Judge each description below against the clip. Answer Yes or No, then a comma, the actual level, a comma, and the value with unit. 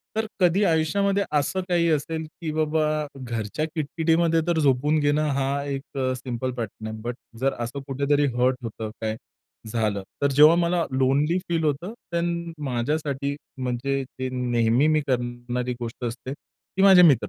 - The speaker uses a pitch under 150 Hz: Yes, medium, 140 Hz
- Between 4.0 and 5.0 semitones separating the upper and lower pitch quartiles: Yes, average, 4.3 semitones